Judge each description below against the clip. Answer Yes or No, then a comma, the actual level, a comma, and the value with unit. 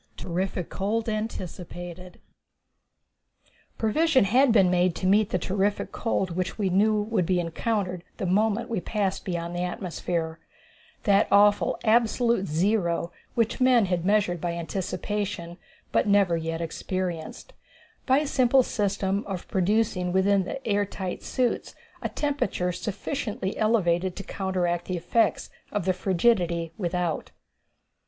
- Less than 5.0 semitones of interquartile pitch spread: Yes, average, 3.4 semitones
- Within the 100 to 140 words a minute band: Yes, slow, 135 wpm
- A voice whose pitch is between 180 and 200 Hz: Yes, high, 190 Hz